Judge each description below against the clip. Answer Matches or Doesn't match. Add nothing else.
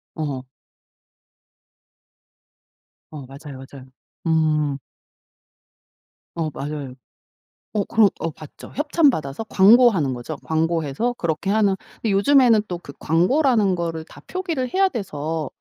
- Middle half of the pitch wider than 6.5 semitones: Matches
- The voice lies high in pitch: Doesn't match